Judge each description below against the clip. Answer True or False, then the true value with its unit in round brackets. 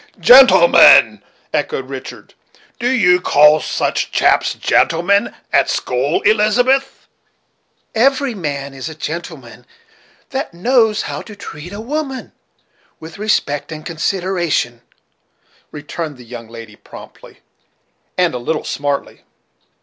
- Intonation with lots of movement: True (7.3 semitones)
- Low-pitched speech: False (170 Hz)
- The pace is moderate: False (110 wpm)